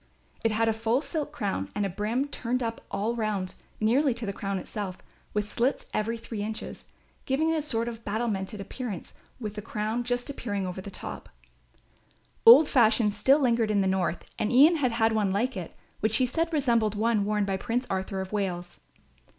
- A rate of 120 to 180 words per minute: No, average, 195 wpm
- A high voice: Yes, high, 220 Hz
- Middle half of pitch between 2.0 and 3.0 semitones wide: No, average, 3.4 semitones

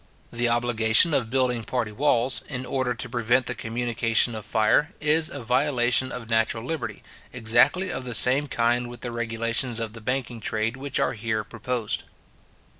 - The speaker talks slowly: No, average, 170 wpm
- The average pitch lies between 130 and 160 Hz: No, low, 120 Hz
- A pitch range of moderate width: No, narrow, 2.3 semitones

